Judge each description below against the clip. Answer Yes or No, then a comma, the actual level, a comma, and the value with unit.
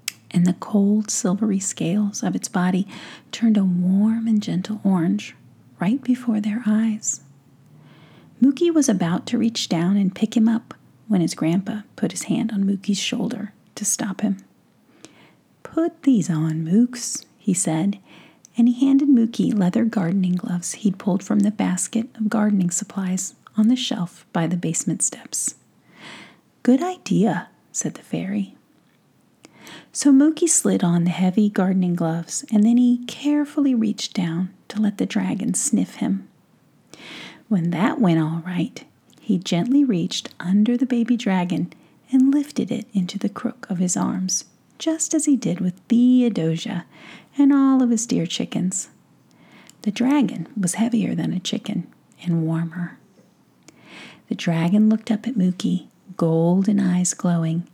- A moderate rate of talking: Yes, average, 150 wpm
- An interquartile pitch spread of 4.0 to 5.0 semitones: Yes, average, 4.5 semitones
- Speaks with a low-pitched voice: No, high, 210 Hz